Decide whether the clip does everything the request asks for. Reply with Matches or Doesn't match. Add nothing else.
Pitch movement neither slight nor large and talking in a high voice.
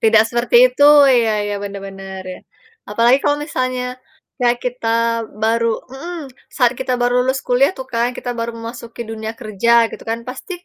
Doesn't match